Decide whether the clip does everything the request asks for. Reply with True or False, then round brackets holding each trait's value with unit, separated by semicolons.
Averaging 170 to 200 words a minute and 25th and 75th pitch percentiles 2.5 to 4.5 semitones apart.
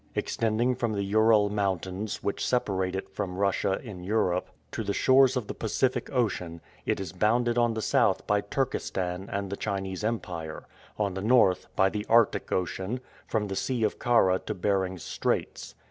True (175 wpm; 3.3 semitones)